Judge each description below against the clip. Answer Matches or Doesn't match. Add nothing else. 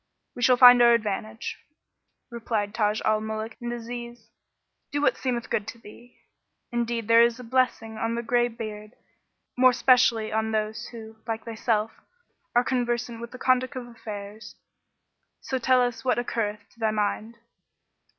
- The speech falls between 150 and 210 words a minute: Matches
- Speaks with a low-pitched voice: Doesn't match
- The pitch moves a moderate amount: Doesn't match